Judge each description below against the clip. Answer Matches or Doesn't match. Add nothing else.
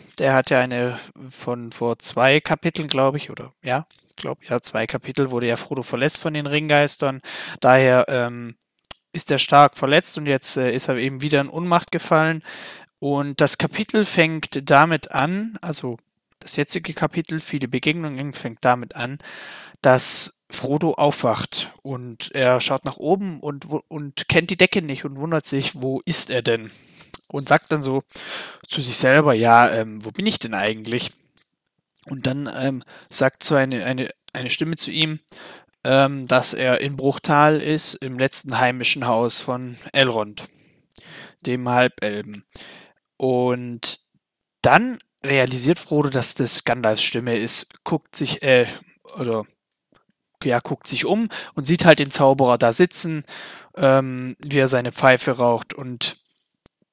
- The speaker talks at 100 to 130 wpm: Doesn't match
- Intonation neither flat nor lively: Matches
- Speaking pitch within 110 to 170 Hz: Matches